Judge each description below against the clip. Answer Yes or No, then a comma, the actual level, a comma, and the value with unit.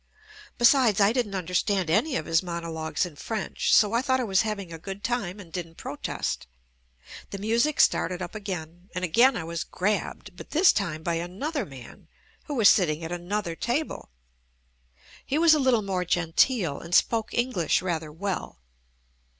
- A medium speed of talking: Yes, average, 180 wpm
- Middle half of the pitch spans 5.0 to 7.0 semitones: Yes, wide, 5.5 semitones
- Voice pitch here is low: No, high, 190 Hz